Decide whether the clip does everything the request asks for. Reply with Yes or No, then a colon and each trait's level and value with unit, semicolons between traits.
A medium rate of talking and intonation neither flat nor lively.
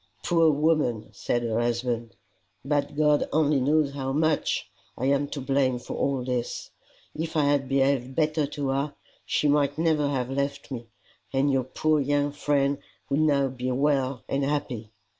No: average, 170 wpm; narrow, 2.1 semitones